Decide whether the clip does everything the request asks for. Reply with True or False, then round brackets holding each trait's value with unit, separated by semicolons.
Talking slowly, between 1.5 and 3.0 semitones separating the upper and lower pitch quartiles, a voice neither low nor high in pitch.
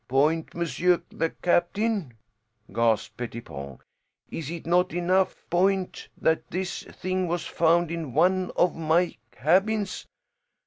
True (120 wpm; 2.6 semitones; 170 Hz)